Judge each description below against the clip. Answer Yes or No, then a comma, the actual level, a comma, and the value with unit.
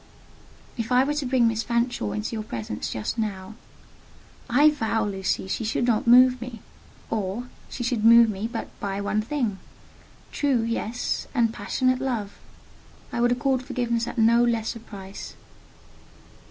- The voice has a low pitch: No, high, 230 Hz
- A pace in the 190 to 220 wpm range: No, average, 155 wpm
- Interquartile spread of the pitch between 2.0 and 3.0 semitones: Yes, average, 2.7 semitones